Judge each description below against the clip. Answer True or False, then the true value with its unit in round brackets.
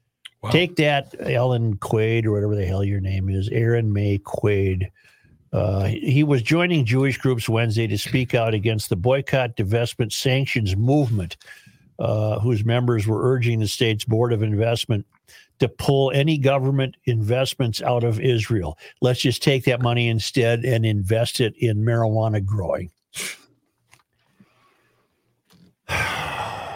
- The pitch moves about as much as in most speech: True (3.2 semitones)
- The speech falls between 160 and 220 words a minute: False (135 wpm)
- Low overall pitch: True (115 Hz)